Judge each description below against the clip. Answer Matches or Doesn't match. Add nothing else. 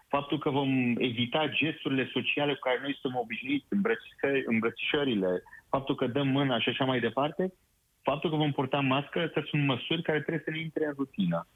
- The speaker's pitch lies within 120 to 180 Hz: Matches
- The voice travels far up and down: Doesn't match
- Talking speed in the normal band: Doesn't match